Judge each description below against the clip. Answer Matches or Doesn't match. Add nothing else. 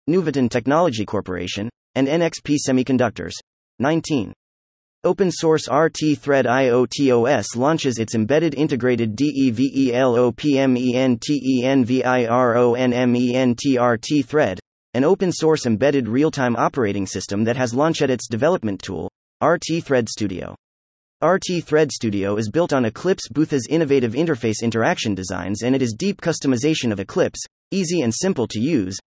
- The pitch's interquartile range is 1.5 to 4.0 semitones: Doesn't match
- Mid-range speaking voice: Doesn't match